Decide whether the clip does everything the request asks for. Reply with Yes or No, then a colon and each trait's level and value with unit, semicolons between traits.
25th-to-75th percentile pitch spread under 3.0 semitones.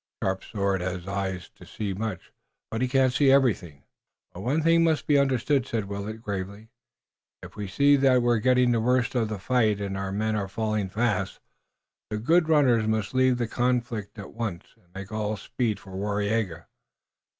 No: average, 4.2 semitones